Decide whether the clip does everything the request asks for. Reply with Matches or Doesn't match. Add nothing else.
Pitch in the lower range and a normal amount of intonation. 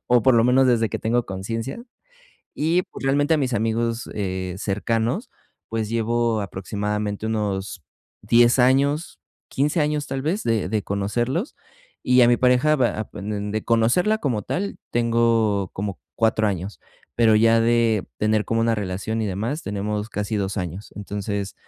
Matches